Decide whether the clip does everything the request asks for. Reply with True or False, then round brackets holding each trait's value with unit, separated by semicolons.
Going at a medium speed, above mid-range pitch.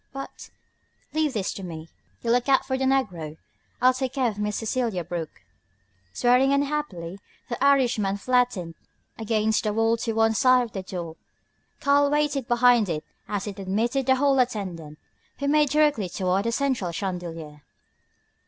True (160 wpm; 230 Hz)